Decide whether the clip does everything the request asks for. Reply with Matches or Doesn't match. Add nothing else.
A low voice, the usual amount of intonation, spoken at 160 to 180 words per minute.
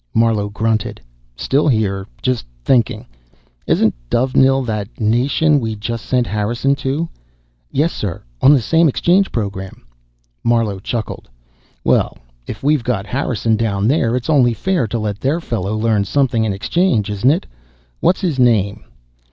Doesn't match